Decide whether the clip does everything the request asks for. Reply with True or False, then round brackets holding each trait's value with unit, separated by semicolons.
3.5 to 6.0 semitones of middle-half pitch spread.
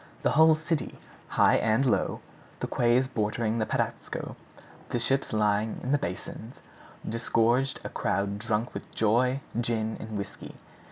False (3.0 semitones)